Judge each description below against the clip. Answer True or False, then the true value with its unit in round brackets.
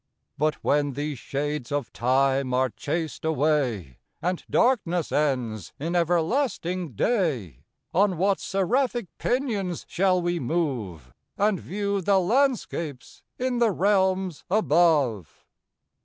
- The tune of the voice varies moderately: False (6.0 semitones)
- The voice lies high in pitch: False (165 Hz)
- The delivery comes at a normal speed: False (110 wpm)